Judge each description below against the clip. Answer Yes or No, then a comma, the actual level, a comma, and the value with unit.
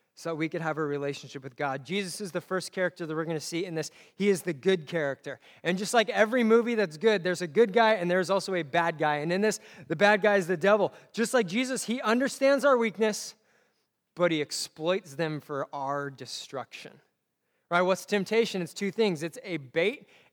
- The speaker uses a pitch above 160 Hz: Yes, medium, 185 Hz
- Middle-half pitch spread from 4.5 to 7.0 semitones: Yes, average, 5.1 semitones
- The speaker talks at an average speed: No, fast, 215 wpm